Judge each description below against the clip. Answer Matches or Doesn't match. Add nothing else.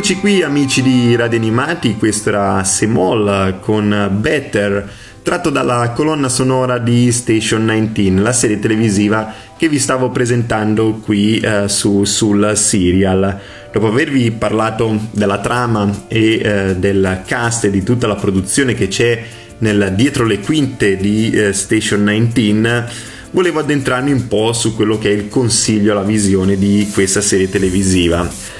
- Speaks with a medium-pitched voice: Doesn't match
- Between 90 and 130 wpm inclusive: Doesn't match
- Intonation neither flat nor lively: Matches